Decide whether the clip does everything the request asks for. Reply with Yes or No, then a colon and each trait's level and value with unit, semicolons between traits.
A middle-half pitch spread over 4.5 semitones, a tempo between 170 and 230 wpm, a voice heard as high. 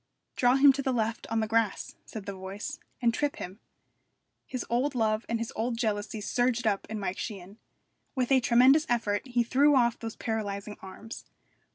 No: average, 2.8 semitones; average, 185 wpm; high, 230 Hz